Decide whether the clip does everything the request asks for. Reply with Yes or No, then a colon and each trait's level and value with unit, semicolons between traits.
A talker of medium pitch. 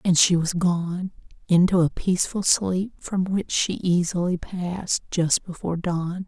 Yes: medium, 180 Hz